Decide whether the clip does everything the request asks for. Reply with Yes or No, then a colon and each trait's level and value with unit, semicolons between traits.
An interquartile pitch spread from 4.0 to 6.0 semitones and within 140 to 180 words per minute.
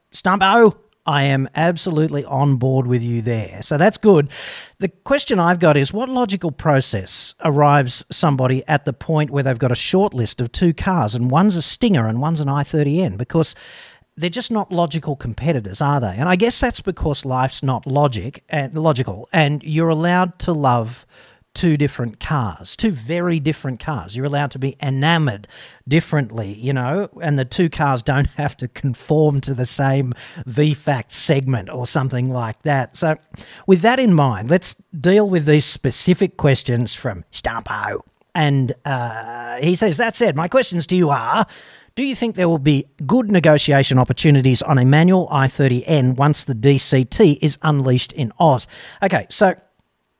Yes: average, 4.6 semitones; average, 170 wpm